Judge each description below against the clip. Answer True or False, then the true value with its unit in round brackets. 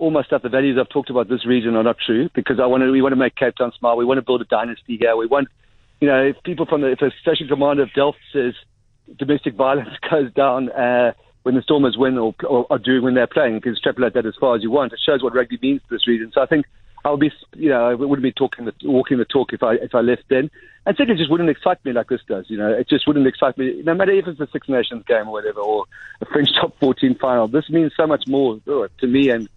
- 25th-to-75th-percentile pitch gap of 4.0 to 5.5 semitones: False (3.1 semitones)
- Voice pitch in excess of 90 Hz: True (130 Hz)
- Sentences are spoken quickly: True (285 wpm)